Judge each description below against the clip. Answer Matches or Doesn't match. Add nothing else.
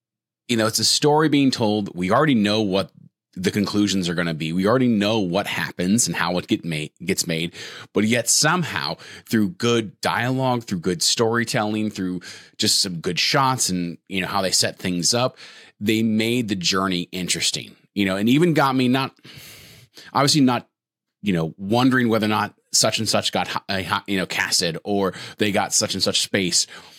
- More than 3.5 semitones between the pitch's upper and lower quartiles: Matches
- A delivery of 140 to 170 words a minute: Doesn't match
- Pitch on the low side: Matches